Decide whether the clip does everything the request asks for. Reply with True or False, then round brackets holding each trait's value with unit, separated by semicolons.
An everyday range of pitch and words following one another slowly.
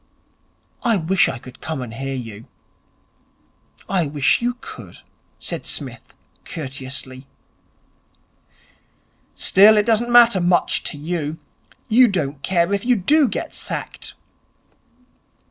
False (8.1 semitones; 115 wpm)